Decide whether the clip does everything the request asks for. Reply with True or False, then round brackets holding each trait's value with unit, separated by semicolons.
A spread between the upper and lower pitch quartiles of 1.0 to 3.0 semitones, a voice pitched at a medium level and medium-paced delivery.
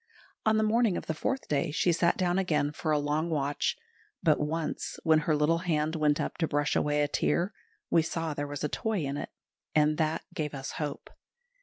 False (2.4 semitones; 155 Hz; 210 wpm)